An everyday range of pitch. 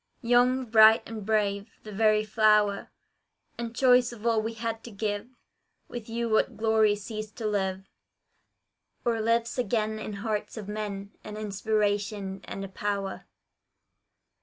No: narrow, 1.8 semitones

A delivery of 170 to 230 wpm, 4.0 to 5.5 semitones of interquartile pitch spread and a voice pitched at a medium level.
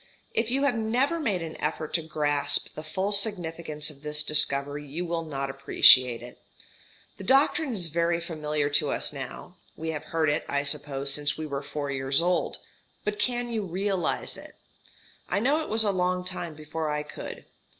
Yes: average, 185 wpm; average, 5.1 semitones; medium, 160 Hz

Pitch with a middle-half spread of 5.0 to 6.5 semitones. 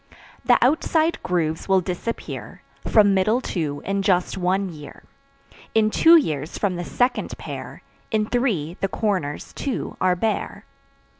No: average, 4.1 semitones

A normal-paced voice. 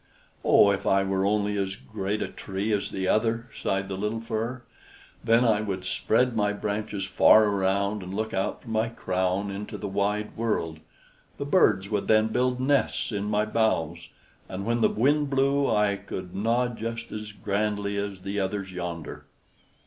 Yes: average, 175 wpm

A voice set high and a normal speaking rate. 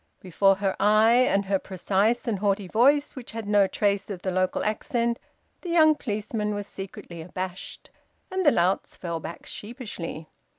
Yes: high, 205 Hz; average, 165 wpm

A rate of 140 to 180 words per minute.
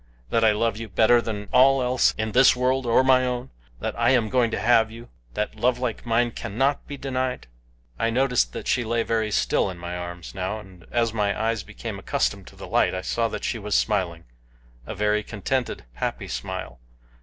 No: fast, 205 wpm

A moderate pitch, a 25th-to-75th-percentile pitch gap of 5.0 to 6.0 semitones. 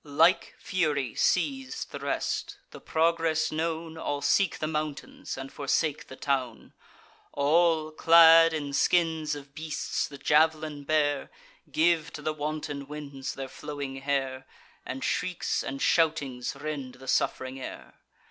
No: medium, 150 Hz; narrow, 2.5 semitones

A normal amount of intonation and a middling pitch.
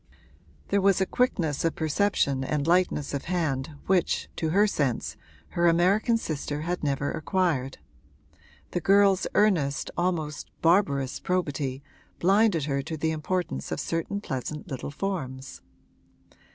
Yes: average, 4.8 semitones; medium, 160 Hz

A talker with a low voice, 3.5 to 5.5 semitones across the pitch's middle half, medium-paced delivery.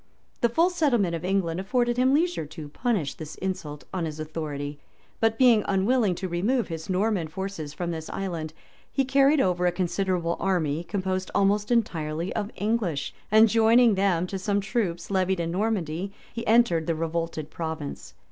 No: high, 190 Hz; average, 5.1 semitones; average, 165 wpm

